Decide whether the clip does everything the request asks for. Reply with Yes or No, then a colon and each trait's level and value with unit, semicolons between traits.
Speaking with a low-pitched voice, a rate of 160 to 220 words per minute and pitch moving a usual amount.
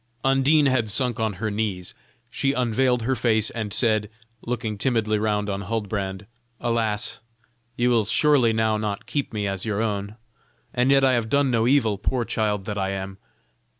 Yes: low, 110 Hz; average, 175 wpm; average, 3.0 semitones